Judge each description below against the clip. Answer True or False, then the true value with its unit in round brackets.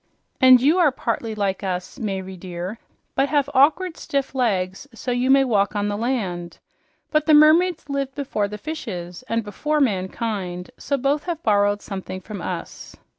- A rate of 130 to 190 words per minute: True (165 wpm)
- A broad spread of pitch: True (6.5 semitones)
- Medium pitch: False (230 Hz)